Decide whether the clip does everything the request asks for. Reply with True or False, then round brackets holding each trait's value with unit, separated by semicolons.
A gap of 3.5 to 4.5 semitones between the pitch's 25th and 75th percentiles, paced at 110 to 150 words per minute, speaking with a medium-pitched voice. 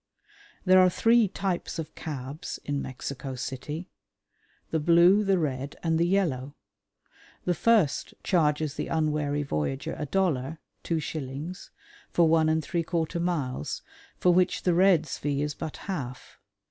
True (3.8 semitones; 145 wpm; 160 Hz)